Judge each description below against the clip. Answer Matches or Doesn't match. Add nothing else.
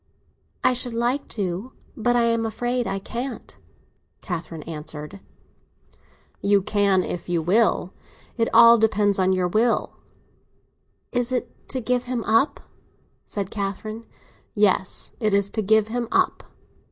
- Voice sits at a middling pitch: Doesn't match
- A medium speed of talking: Doesn't match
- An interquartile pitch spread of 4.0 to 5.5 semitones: Doesn't match